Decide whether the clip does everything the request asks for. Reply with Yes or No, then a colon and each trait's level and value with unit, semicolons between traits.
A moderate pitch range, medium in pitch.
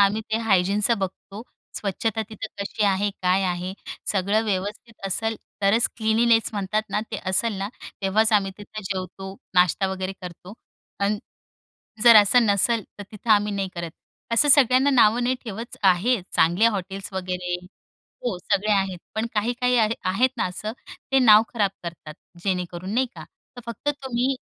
No: average, 3.1 semitones; high, 205 Hz